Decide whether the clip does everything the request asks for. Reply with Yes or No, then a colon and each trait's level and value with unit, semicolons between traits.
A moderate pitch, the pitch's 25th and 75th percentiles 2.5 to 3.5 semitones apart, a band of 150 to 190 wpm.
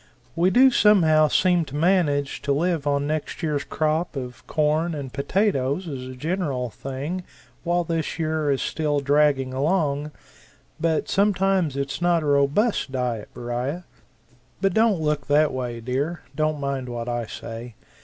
No: medium, 150 Hz; average, 4.1 semitones; average, 155 wpm